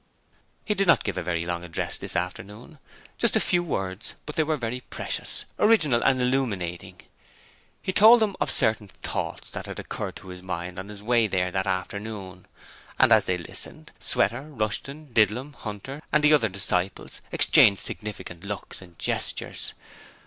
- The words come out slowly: No, average, 170 wpm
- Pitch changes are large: Yes, wide, 6.7 semitones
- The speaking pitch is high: No, low, 105 Hz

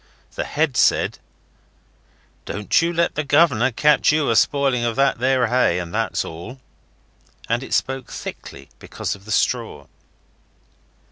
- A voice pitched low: Yes, low, 130 Hz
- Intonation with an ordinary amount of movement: Yes, average, 4.2 semitones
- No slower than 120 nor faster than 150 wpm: Yes, average, 140 wpm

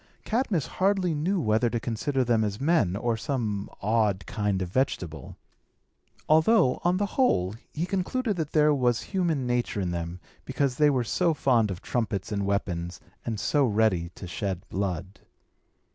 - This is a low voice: Yes, low, 120 Hz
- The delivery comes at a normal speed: Yes, average, 160 wpm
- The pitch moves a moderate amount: No, wide, 7.7 semitones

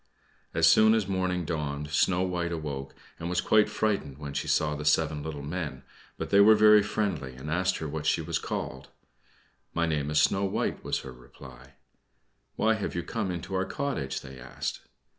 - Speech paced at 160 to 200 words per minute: Yes, average, 190 wpm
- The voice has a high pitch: No, very low, 80 Hz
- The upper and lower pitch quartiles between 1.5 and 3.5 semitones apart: No, average, 4.7 semitones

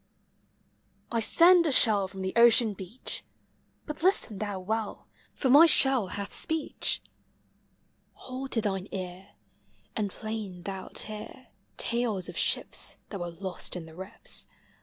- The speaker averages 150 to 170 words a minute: No, average, 140 wpm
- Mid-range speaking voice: No, high, 210 Hz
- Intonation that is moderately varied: Yes, average, 4.8 semitones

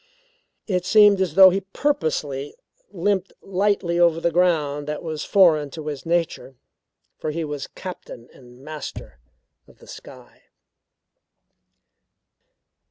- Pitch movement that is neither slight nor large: Yes, average, 4.2 semitones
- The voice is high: No, medium, 170 Hz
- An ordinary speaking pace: No, slow, 120 wpm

